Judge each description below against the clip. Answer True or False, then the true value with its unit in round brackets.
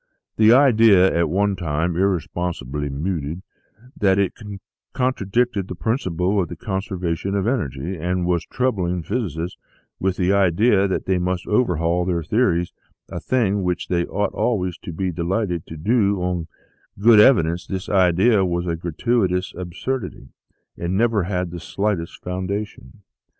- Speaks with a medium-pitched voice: False (95 Hz)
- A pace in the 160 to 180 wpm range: False (145 wpm)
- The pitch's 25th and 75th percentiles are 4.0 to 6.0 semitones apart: False (3.1 semitones)